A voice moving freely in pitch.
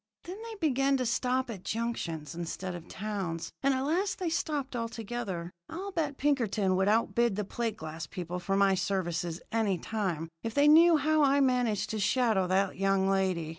Yes: wide, 6.5 semitones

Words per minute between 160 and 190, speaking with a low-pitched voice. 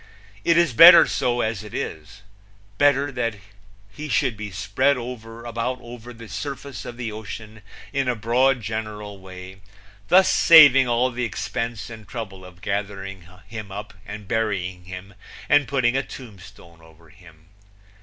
No: average, 150 wpm; low, 110 Hz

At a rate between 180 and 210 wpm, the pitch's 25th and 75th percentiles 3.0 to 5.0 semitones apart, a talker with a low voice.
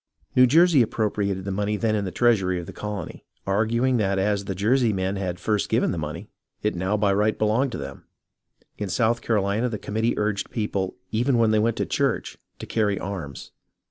No: average, 200 wpm; narrow, 2.6 semitones; low, 105 Hz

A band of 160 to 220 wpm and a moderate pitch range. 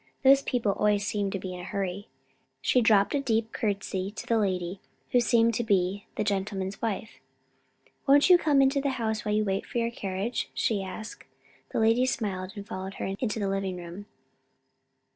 Yes: average, 190 wpm; average, 3.2 semitones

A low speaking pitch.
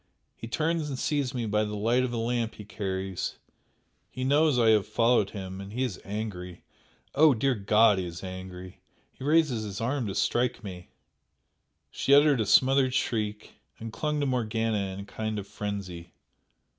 Yes: low, 110 Hz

